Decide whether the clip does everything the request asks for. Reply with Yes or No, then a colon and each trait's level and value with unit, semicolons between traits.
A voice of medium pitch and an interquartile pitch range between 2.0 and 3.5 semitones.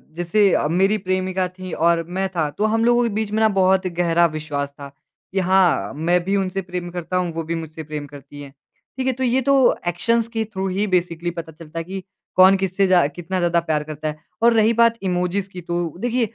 Yes: medium, 180 Hz; average, 2.9 semitones